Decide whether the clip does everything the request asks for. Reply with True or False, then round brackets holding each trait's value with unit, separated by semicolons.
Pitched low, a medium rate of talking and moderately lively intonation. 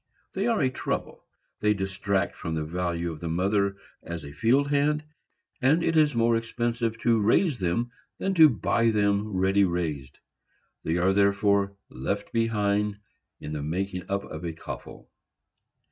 True (100 Hz; 160 wpm; 4.7 semitones)